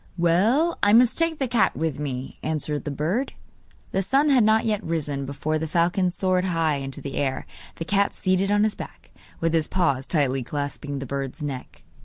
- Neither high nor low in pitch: Yes, medium, 165 Hz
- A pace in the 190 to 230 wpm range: Yes, average, 195 wpm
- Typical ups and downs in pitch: No, wide, 6.1 semitones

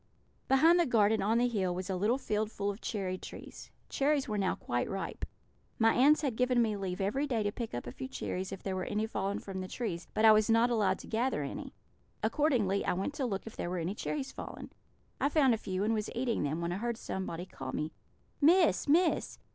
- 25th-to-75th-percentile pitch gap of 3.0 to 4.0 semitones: No, average, 4.8 semitones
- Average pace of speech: No, fast, 235 wpm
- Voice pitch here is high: Yes, high, 215 Hz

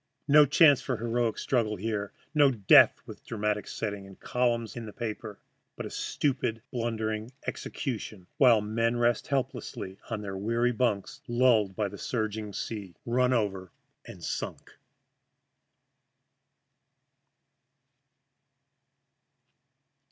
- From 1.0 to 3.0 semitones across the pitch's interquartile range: Yes, average, 2.7 semitones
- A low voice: Yes, low, 115 Hz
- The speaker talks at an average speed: No, slow, 115 wpm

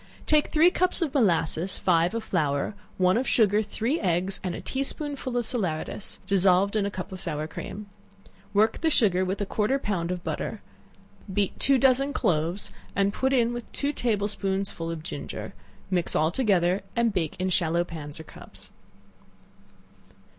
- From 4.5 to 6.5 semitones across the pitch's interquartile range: Yes, wide, 5.4 semitones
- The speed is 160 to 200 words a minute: Yes, average, 175 wpm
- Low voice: No, high, 195 Hz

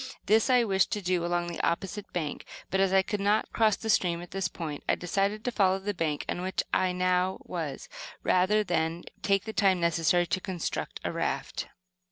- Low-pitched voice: No, medium, 185 Hz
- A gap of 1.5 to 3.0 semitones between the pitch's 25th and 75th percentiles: Yes, narrow, 2.5 semitones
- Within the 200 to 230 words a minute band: Yes, fast, 205 wpm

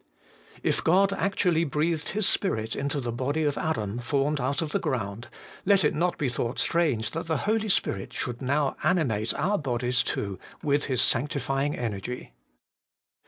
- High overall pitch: No, medium, 140 Hz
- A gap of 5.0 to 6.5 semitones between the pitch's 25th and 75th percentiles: Yes, average, 5.3 semitones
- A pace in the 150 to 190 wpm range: Yes, average, 165 wpm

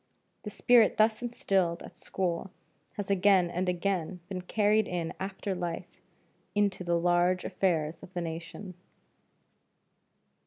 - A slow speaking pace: Yes, slow, 125 wpm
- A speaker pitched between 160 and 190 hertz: Yes, medium, 185 Hz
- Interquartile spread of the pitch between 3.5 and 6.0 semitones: No, narrow, 2.5 semitones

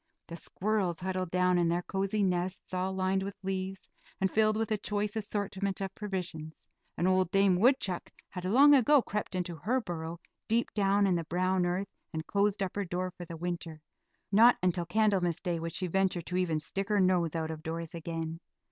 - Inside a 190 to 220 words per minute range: Yes, average, 195 wpm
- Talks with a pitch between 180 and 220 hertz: Yes, medium, 185 Hz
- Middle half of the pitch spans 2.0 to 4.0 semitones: Yes, narrow, 2.6 semitones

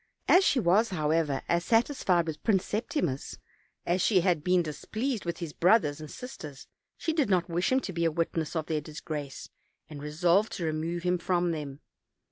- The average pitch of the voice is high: No, medium, 170 Hz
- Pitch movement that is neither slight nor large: Yes, average, 3.8 semitones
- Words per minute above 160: Yes, average, 195 wpm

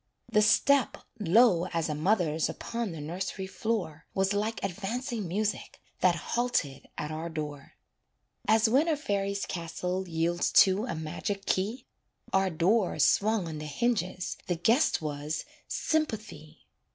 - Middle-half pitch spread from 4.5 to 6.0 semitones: Yes, average, 5.1 semitones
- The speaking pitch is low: No, high, 190 Hz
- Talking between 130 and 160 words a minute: Yes, average, 140 wpm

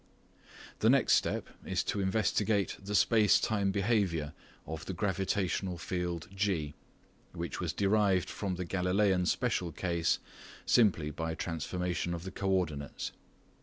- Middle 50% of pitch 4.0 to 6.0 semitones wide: No, average, 2.9 semitones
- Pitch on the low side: Yes, very low, 95 Hz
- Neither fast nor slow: No, slow, 130 wpm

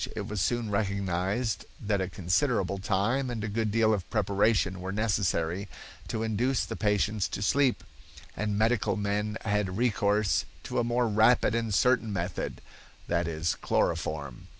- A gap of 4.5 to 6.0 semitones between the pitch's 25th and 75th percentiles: No, average, 2.8 semitones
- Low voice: Yes, low, 105 Hz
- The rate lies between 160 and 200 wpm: No, average, 150 wpm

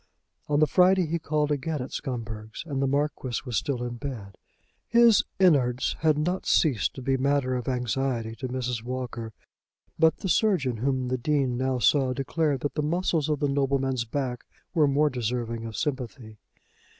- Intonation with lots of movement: No, average, 3.4 semitones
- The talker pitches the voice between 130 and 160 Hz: Yes, low, 135 Hz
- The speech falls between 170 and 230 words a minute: Yes, average, 175 wpm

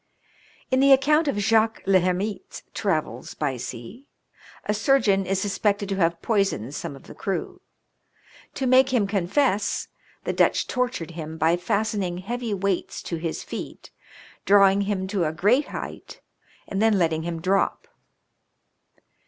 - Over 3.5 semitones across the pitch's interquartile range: Yes, average, 4.3 semitones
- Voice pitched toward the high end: Yes, high, 195 Hz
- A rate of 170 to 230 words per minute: No, average, 145 wpm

